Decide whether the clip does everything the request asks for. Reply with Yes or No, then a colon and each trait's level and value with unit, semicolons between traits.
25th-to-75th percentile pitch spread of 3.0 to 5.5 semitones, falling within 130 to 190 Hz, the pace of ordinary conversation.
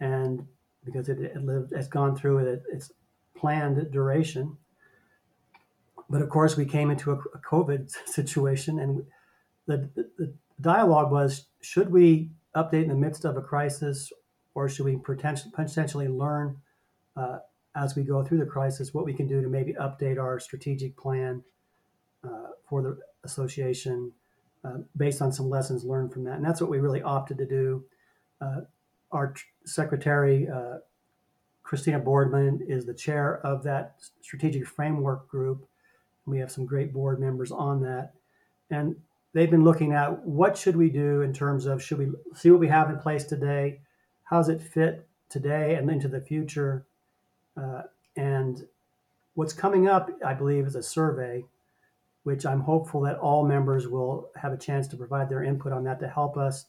No: narrow, 2.4 semitones; medium, 140 Hz; average, 170 wpm